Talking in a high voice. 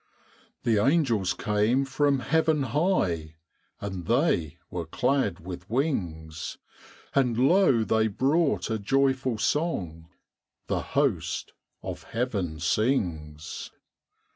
No: low, 115 Hz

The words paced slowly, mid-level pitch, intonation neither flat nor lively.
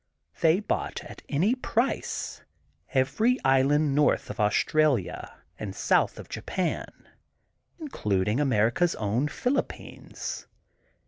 No: slow, 105 wpm; medium, 145 Hz; wide, 7.8 semitones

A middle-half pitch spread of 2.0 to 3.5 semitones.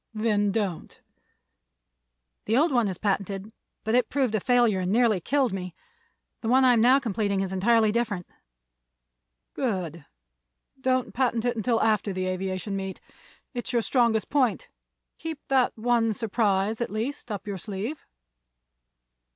No: average, 3.9 semitones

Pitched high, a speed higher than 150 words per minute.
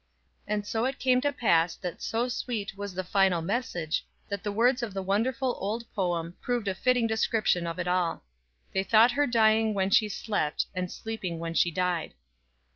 Yes: high, 205 Hz; average, 190 wpm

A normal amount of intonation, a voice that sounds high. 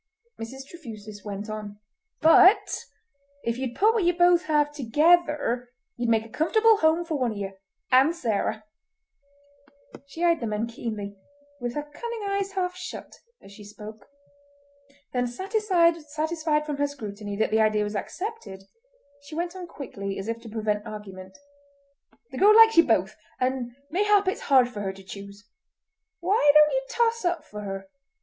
No: wide, 8.3 semitones; very high, 260 Hz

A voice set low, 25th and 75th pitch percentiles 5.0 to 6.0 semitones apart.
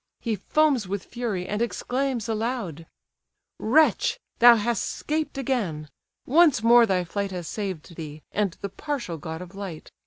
No: high, 210 Hz; average, 5.3 semitones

